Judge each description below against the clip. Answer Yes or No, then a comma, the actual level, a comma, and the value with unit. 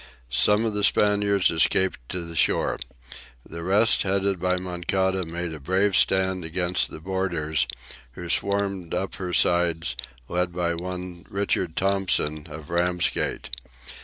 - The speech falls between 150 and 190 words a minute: No, slow, 135 wpm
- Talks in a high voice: No, very low, 90 Hz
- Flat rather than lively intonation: Yes, narrow, 2.2 semitones